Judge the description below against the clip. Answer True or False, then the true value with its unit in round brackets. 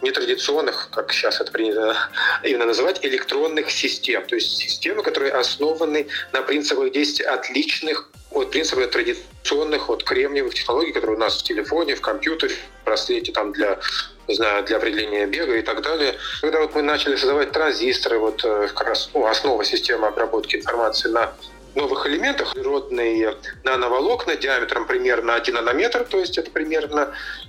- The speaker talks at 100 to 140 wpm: False (150 wpm)